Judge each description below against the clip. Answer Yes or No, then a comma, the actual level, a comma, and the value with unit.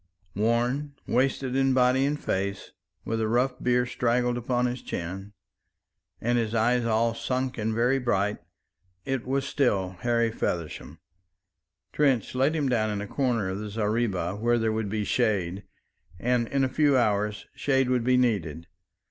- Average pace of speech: Yes, average, 160 wpm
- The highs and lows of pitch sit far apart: No, average, 3.3 semitones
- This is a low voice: Yes, low, 120 Hz